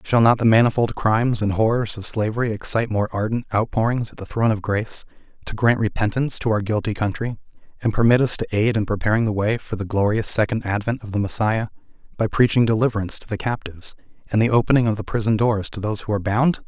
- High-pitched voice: No, low, 110 Hz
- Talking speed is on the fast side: Yes, fast, 215 wpm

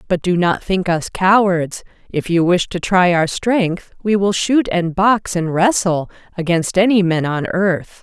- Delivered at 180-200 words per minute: Yes, average, 185 wpm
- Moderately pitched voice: Yes, medium, 180 Hz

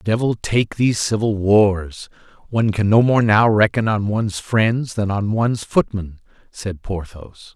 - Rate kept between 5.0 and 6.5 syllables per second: No, 4.3 syllables/s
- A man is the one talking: Yes, male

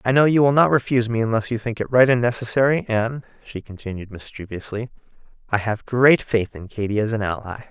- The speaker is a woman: No, male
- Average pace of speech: No, fast, 210 wpm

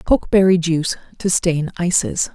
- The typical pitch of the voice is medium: Yes, medium, 175 Hz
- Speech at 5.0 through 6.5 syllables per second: Yes, 5.1 syllables/s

